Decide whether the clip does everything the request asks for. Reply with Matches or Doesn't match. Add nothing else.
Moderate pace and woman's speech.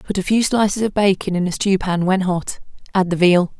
Doesn't match